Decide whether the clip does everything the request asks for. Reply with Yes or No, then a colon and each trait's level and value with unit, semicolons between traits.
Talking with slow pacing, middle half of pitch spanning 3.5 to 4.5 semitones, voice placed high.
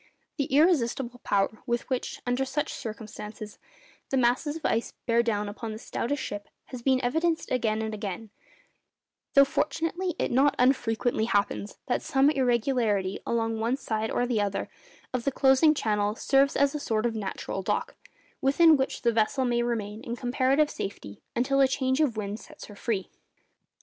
No: average, 170 wpm; average, 3.8 semitones; high, 240 Hz